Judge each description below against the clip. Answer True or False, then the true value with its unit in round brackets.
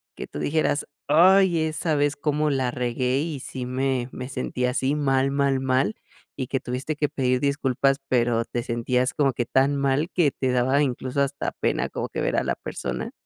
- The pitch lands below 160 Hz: True (135 Hz)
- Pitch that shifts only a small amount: True (2.3 semitones)